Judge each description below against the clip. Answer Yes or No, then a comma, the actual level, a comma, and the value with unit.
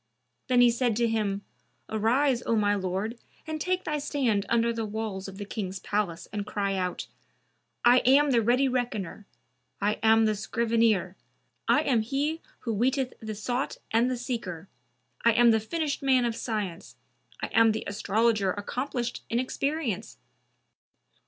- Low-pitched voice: No, high, 225 Hz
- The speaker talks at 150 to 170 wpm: Yes, average, 160 wpm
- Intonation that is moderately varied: Yes, average, 3.4 semitones